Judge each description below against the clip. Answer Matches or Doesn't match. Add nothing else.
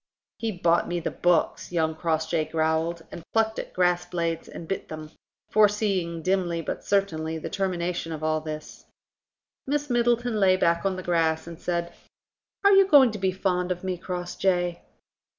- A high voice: Doesn't match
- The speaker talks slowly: Doesn't match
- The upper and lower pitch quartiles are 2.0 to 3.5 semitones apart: Matches